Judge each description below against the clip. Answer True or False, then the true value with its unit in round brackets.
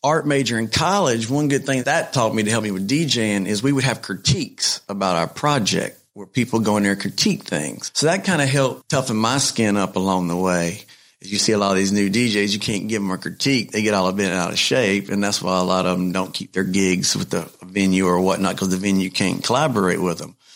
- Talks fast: True (260 wpm)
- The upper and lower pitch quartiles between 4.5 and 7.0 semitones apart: False (4.0 semitones)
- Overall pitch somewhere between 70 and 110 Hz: True (100 Hz)